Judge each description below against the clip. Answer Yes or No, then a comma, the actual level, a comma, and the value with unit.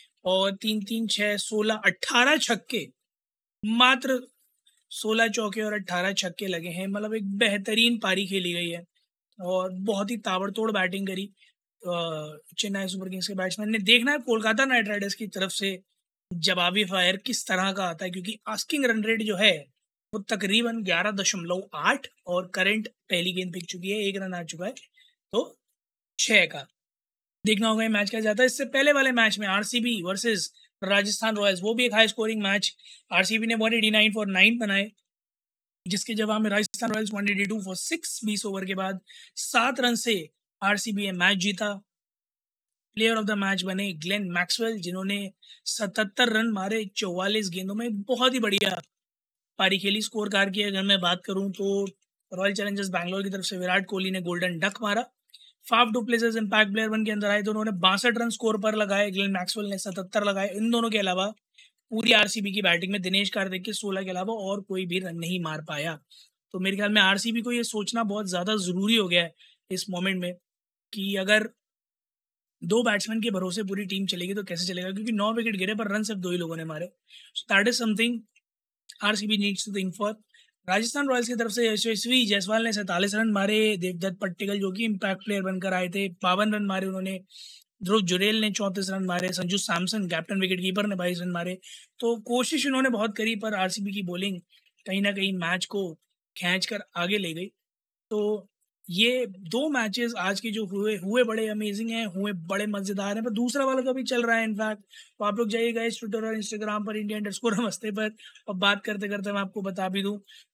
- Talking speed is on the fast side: Yes, fast, 195 wpm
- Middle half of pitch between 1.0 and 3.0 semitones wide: Yes, average, 2.7 semitones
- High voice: Yes, high, 205 Hz